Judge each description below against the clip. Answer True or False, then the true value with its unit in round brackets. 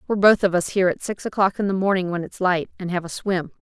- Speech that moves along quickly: True (295 wpm)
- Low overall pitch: False (190 Hz)